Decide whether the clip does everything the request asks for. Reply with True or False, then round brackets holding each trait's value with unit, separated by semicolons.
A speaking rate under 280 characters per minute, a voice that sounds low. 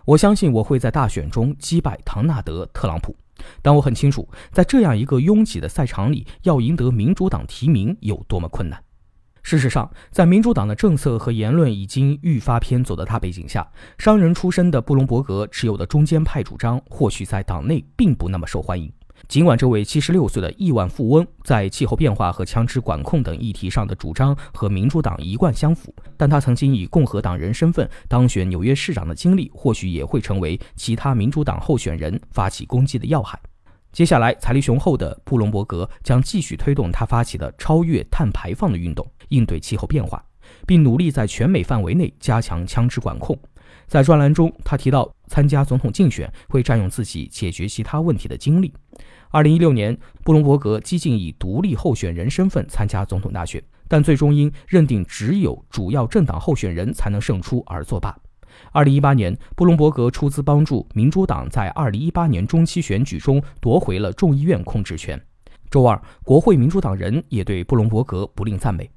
False (300 characters per minute; 125 Hz)